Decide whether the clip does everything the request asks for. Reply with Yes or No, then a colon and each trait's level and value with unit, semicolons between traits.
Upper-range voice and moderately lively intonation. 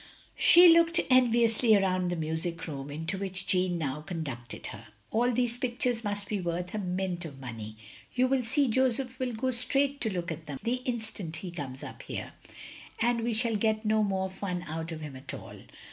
No: high, 195 Hz; wide, 6.5 semitones